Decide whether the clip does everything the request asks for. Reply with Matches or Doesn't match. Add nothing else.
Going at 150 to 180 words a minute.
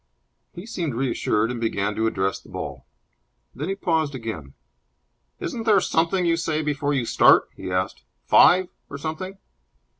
Matches